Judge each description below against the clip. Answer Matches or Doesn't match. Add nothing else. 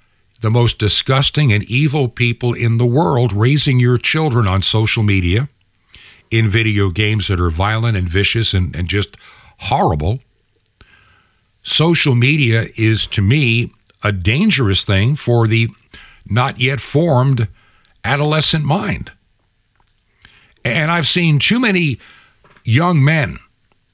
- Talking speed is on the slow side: Matches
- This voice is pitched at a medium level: Doesn't match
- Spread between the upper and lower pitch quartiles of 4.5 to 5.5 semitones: Matches